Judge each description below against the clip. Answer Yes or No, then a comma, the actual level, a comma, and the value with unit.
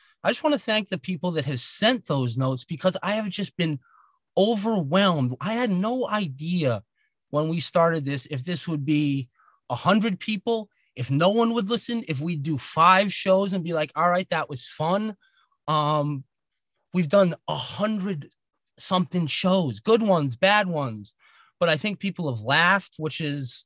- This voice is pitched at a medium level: Yes, medium, 175 Hz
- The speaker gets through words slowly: No, average, 180 wpm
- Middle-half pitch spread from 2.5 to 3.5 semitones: No, average, 5.2 semitones